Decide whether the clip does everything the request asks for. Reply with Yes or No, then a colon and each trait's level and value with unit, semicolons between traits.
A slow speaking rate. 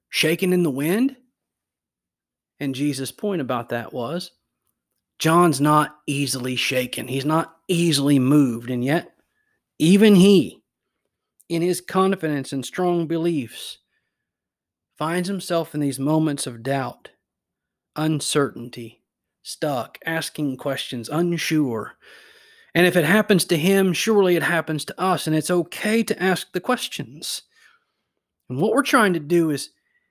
Yes: slow, 130 wpm